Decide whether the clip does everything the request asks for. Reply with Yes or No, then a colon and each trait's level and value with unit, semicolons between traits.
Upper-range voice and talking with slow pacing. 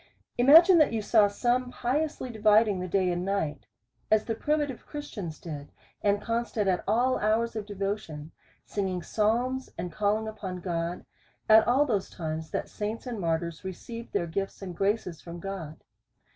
No: high, 205 Hz; average, 160 wpm